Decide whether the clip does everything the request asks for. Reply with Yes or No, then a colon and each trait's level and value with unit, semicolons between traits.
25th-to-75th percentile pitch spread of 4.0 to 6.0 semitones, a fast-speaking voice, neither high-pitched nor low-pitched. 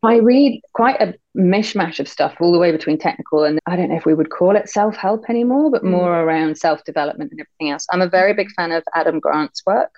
Yes: average, 4.5 semitones; fast, 245 wpm; medium, 175 Hz